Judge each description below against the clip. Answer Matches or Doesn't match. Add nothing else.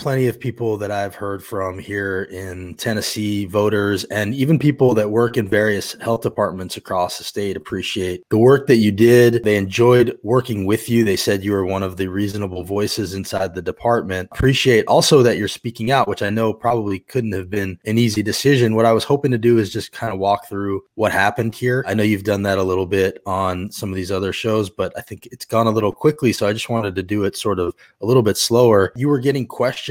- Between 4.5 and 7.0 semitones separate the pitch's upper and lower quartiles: Doesn't match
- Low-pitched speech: Matches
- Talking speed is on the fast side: Matches